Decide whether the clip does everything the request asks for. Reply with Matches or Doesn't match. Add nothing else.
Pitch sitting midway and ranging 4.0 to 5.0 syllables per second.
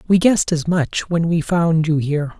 Matches